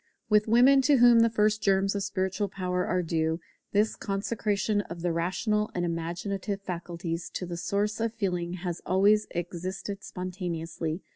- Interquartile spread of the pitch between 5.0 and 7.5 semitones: No, average, 3.3 semitones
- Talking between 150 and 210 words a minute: Yes, average, 155 wpm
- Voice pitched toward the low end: No, high, 190 Hz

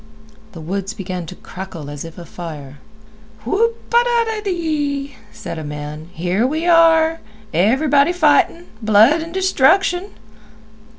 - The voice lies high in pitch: Yes, very high, 270 Hz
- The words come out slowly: Yes, slow, 120 wpm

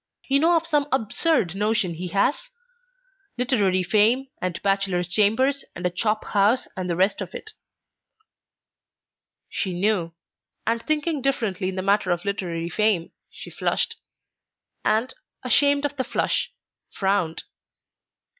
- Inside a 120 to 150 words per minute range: Yes, slow, 135 wpm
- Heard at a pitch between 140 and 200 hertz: No, high, 210 Hz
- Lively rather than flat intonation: Yes, wide, 6.0 semitones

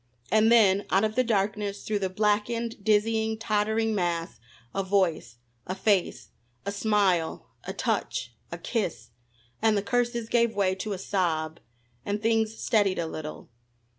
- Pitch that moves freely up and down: No, average, 2.8 semitones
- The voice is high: Yes, high, 205 Hz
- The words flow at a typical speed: Yes, average, 150 wpm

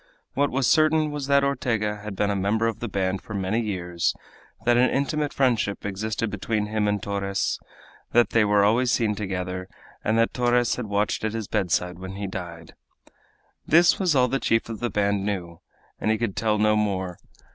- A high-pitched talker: No, low, 105 Hz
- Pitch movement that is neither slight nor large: Yes, average, 3.5 semitones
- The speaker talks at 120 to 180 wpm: No, average, 195 wpm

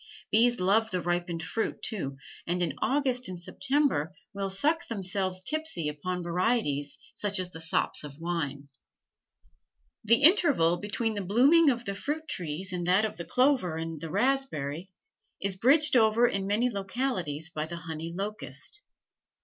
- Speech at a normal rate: Yes, average, 155 wpm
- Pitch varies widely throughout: Yes, wide, 6.3 semitones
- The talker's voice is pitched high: Yes, high, 195 Hz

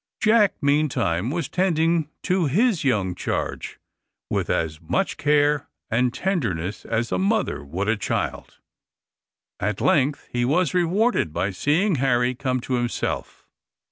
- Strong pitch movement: Yes, wide, 7.3 semitones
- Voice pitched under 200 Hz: Yes, medium, 140 Hz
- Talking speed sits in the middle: No, slow, 130 wpm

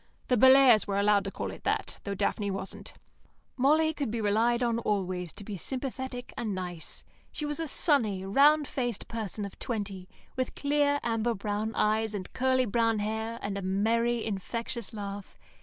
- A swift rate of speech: No, average, 175 wpm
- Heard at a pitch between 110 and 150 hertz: No, high, 220 Hz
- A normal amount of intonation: Yes, average, 4.1 semitones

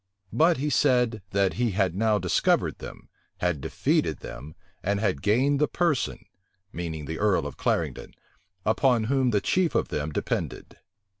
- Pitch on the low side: Yes, low, 105 Hz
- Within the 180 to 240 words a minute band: No, average, 155 wpm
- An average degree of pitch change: No, wide, 6.8 semitones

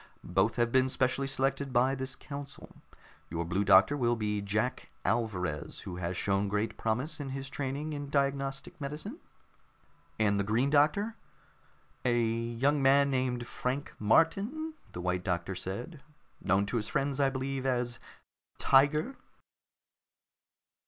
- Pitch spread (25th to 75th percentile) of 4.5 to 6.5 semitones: Yes, average, 4.9 semitones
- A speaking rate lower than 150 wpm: Yes, average, 140 wpm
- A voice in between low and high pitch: No, low, 130 Hz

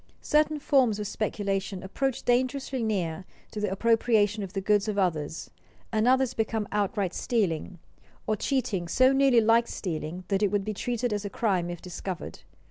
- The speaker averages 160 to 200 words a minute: Yes, average, 170 wpm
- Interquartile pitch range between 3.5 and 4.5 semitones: Yes, average, 3.9 semitones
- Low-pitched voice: No, high, 210 Hz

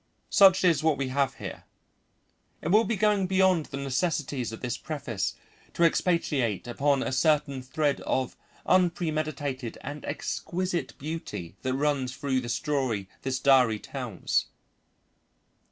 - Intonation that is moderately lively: Yes, average, 4.2 semitones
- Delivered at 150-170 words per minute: No, slow, 135 wpm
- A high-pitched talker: No, medium, 140 Hz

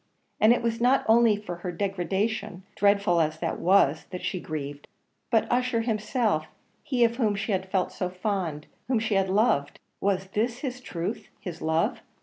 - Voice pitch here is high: Yes, high, 200 Hz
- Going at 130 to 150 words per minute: No, average, 185 wpm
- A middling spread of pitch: Yes, average, 4.4 semitones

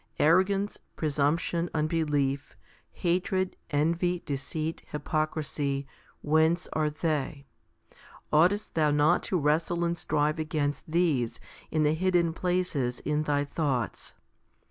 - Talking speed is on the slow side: Yes, slow, 105 wpm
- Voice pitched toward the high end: No, medium, 155 Hz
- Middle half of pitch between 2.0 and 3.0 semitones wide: Yes, narrow, 2.6 semitones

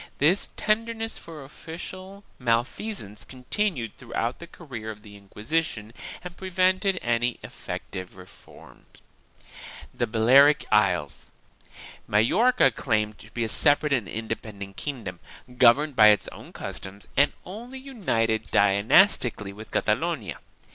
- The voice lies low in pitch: Yes, low, 125 Hz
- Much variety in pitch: Yes, wide, 8.7 semitones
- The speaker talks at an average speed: No, slow, 115 wpm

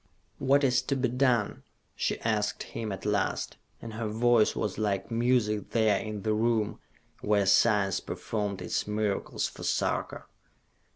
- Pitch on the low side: Yes, low, 110 Hz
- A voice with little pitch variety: Yes, narrow, 2.2 semitones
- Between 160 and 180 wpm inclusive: No, average, 150 wpm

